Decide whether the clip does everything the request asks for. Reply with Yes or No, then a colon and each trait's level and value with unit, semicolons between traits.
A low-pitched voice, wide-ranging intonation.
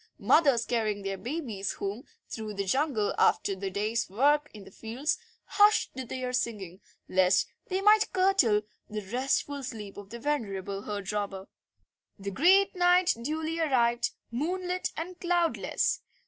No: high, 240 Hz; wide, 7.9 semitones